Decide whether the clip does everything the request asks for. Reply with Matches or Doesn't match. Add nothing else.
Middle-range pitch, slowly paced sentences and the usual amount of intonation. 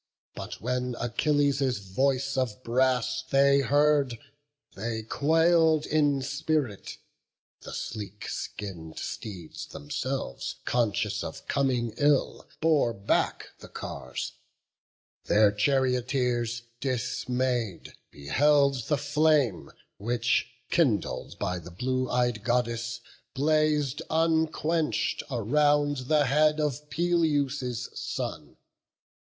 Doesn't match